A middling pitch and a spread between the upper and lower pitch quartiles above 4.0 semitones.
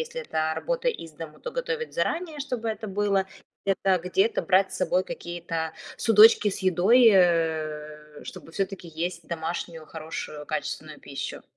Yes: medium, 180 Hz; average, 5.3 semitones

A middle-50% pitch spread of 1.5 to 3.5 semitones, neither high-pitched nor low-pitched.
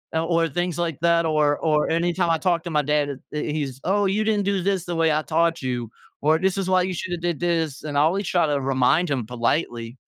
Yes: average, 3.1 semitones; medium, 165 Hz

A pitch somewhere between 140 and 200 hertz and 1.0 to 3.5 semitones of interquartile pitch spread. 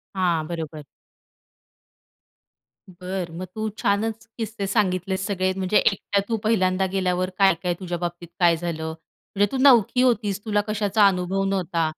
Yes: high, 190 Hz; average, 2.9 semitones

